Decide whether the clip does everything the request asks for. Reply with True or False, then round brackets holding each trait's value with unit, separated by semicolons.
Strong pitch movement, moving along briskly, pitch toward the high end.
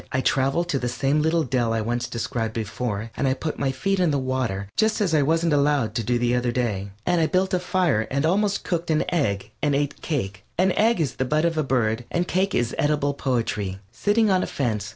False (5.8 semitones; 235 wpm; 140 Hz)